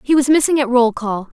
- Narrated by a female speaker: Yes, female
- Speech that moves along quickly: Yes, fast, 260 wpm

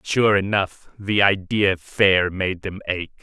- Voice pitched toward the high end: No, very low, 95 Hz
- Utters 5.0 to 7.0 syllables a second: No, 3.5 syllables/s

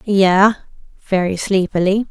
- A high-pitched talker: Yes, high, 195 Hz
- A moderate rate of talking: No, slow, 85 wpm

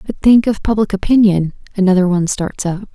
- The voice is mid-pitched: No, high, 200 Hz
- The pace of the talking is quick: No, average, 185 wpm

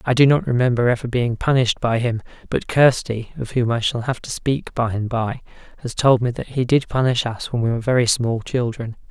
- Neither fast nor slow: No, fast, 230 wpm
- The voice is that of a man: Yes, male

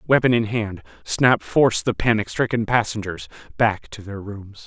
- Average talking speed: Yes, average, 165 wpm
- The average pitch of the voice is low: Yes, low, 105 Hz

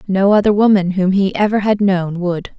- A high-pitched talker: Yes, high, 195 Hz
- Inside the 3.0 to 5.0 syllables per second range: Yes, 4.9 syllables/s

